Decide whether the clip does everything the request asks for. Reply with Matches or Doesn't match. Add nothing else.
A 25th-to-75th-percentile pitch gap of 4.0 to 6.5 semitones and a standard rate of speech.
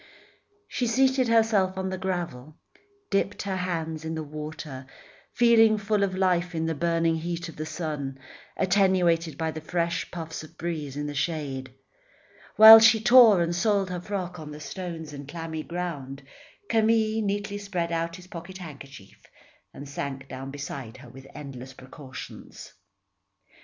Matches